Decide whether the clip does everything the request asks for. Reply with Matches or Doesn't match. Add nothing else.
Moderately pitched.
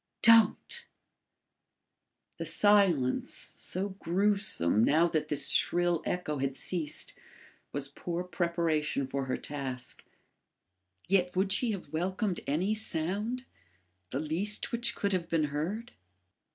Matches